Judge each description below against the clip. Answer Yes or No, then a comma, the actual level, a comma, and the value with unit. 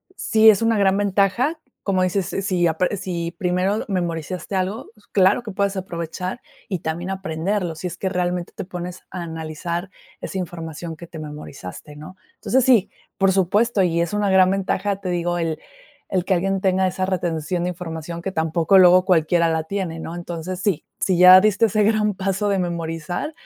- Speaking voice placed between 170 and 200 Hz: Yes, medium, 185 Hz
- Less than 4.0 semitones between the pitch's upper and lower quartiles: Yes, narrow, 2.5 semitones